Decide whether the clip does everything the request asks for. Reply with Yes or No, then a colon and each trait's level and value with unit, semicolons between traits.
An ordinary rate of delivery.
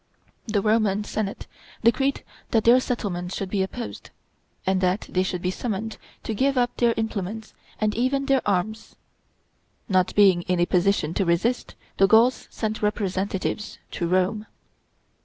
Yes: average, 150 wpm